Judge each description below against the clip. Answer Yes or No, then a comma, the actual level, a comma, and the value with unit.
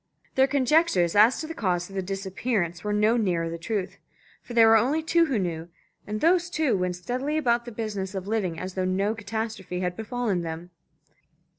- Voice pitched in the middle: No, high, 210 Hz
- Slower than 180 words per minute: No, average, 200 wpm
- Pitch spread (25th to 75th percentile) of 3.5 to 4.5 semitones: No, average, 5.1 semitones